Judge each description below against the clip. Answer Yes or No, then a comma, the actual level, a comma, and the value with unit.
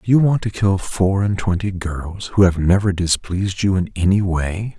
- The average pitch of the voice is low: Yes, very low, 95 Hz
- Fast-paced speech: Yes, fast, 215 wpm